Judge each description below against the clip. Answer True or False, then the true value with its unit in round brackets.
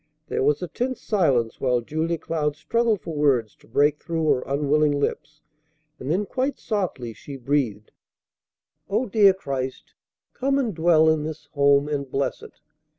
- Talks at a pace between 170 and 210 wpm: False (160 wpm)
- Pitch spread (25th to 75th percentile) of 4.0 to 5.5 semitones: True (4.9 semitones)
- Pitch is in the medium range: True (150 Hz)